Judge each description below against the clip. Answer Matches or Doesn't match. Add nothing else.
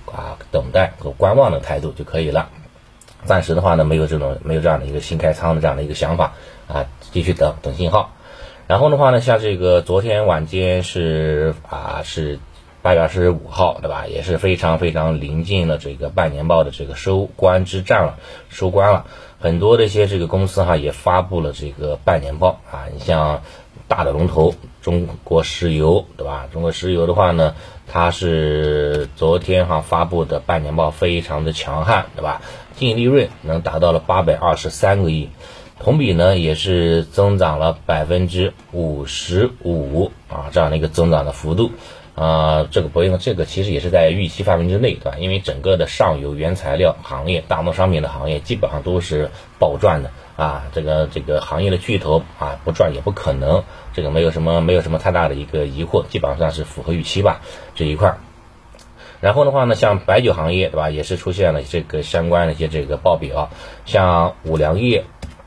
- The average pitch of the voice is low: Matches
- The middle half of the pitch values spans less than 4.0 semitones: Matches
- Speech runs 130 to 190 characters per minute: Doesn't match